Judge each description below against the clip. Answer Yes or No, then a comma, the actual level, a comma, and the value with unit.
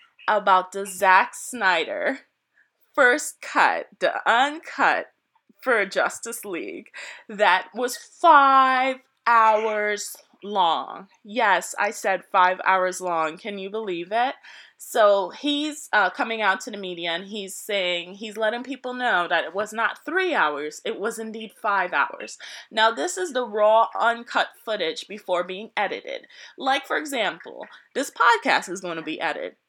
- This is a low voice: No, high, 220 Hz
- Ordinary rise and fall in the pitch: No, wide, 5.7 semitones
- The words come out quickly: No, average, 145 wpm